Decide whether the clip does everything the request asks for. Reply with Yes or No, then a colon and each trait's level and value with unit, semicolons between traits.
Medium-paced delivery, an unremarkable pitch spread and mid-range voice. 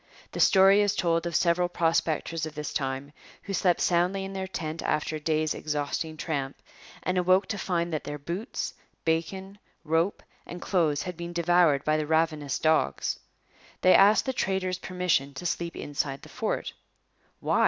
Yes: average, 170 wpm; average, 3.1 semitones; medium, 170 Hz